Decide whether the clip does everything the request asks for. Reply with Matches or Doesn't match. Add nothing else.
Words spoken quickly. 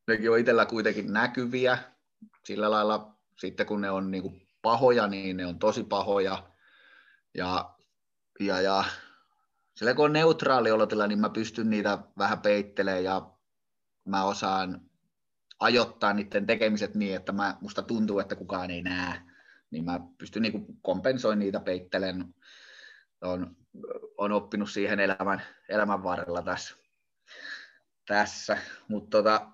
Doesn't match